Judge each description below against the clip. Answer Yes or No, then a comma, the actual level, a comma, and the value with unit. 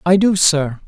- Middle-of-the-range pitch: Yes, medium, 170 Hz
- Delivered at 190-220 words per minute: Yes, fast, 205 wpm